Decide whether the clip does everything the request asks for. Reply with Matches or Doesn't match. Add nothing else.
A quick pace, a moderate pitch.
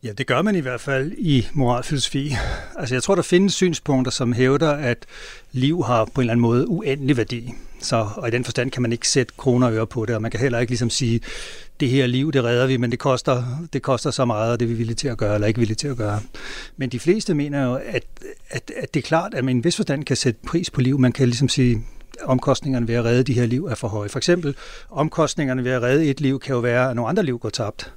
Doesn't match